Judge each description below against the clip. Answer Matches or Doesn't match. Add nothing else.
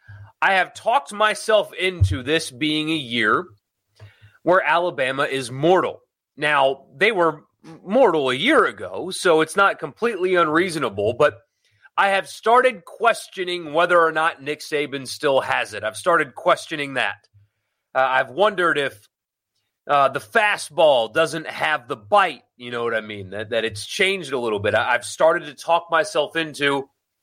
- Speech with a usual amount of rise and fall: Doesn't match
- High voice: Doesn't match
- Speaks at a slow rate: Doesn't match